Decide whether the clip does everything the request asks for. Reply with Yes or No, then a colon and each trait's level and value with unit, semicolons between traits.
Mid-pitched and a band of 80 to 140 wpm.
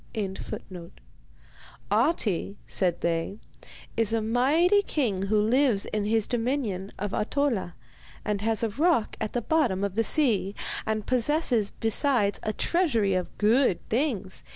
No: high, 220 Hz; slow, 135 wpm